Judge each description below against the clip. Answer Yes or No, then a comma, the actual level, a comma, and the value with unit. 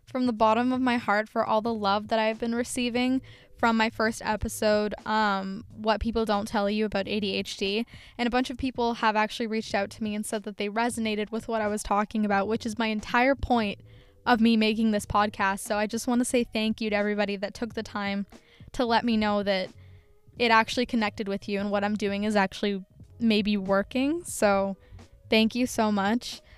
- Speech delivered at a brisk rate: Yes, fast, 215 wpm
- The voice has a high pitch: Yes, high, 215 Hz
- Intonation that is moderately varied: No, narrow, 2.2 semitones